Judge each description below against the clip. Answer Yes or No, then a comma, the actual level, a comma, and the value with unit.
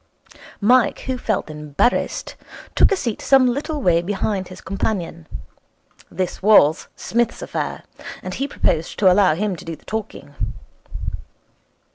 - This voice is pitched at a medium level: No, high, 200 Hz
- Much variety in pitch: Yes, wide, 6.0 semitones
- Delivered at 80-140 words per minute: Yes, slow, 135 wpm